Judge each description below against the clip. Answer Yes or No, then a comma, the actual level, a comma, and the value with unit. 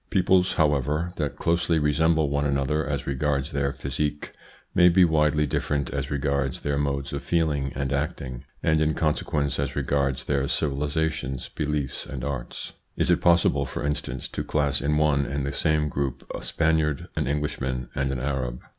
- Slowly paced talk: No, average, 170 wpm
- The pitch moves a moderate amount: No, narrow, 1.8 semitones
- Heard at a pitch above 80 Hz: No, very low, 70 Hz